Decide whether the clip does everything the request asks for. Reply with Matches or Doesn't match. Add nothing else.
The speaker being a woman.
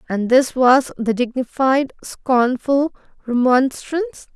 Matches